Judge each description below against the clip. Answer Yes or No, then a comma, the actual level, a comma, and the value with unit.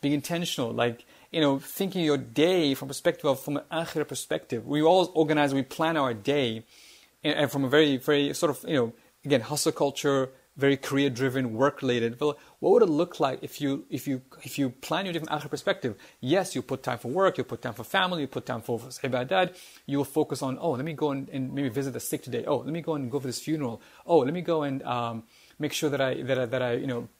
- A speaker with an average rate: No, fast, 250 wpm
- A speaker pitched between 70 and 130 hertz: No, medium, 140 Hz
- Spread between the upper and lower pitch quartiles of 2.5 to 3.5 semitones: Yes, average, 3.0 semitones